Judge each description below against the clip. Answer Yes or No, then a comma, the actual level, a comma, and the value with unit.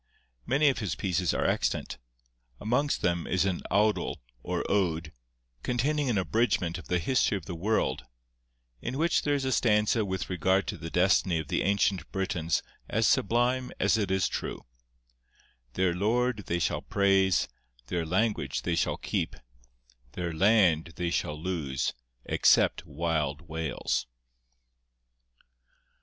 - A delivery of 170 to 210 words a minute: No, average, 140 wpm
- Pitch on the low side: Yes, very low, 95 Hz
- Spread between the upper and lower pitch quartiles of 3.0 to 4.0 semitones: No, average, 4.6 semitones